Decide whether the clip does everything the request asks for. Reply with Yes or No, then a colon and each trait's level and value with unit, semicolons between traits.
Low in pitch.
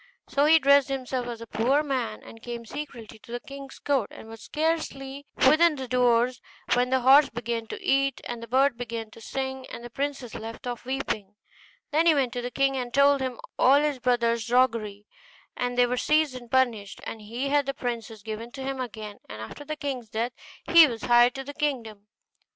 No: very high, 250 Hz